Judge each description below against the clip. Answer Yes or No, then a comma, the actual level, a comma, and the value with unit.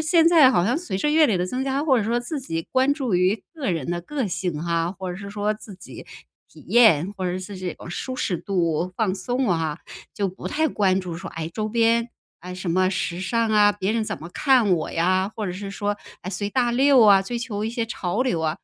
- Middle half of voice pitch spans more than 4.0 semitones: Yes, average, 5.0 semitones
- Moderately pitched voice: No, high, 205 Hz